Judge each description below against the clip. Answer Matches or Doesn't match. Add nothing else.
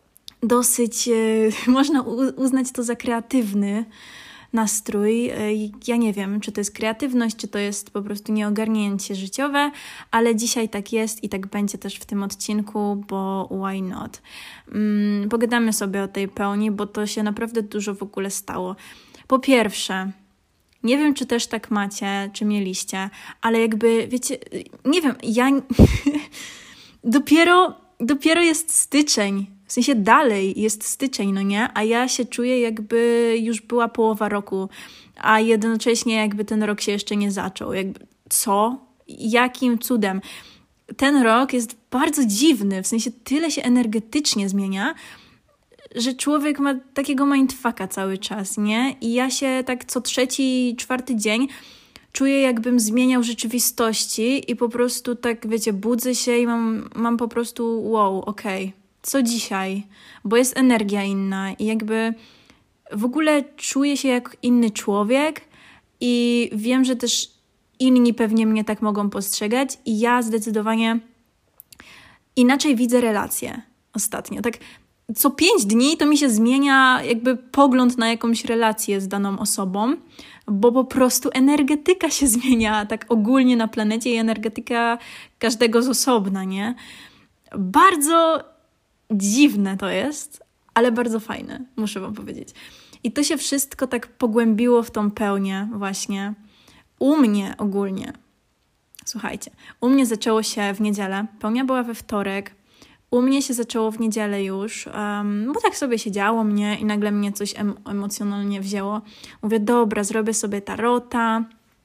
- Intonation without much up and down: Doesn't match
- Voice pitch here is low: Doesn't match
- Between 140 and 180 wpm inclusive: Matches